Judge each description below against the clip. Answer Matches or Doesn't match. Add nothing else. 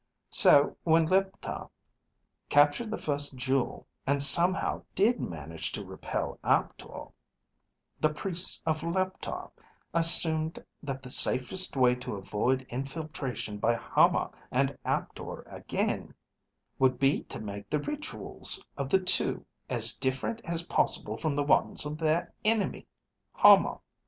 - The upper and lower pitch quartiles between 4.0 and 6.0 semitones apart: Matches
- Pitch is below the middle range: Doesn't match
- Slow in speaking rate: Matches